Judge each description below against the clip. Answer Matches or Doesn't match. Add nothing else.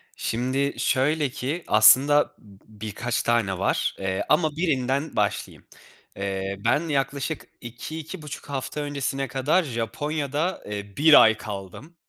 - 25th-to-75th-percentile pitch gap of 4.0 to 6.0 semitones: Matches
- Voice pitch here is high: Doesn't match